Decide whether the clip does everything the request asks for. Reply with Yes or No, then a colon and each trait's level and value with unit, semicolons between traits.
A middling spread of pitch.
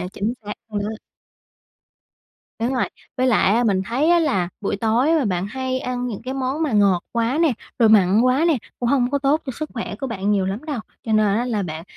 Yes: average, 4.4 semitones